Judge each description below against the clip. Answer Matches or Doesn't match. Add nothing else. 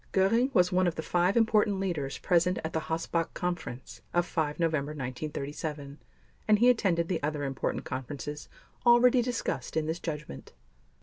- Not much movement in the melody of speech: Doesn't match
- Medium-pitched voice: Matches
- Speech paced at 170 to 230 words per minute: Doesn't match